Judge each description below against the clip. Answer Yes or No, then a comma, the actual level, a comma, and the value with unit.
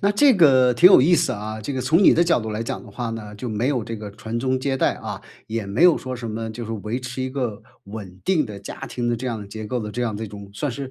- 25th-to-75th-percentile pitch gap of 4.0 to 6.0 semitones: No, average, 3.4 semitones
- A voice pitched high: No, low, 120 Hz